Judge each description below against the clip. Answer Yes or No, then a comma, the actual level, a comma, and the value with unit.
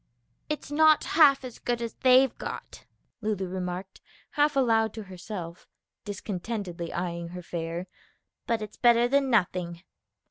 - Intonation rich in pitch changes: Yes, wide, 5.9 semitones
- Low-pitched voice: No, high, 215 Hz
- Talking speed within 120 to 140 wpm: Yes, slow, 135 wpm